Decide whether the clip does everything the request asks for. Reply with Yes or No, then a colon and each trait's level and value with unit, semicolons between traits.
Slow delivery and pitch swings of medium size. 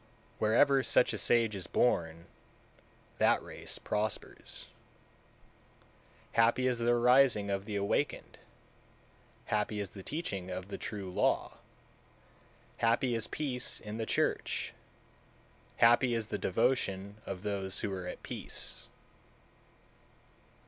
Yes: slow, 120 wpm; average, 3.5 semitones